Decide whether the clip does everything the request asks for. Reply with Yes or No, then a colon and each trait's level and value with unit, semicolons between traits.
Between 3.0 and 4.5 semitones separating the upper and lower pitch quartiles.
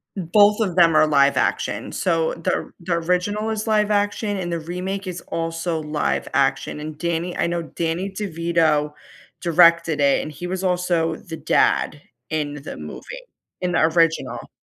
No: narrow, 2.4 semitones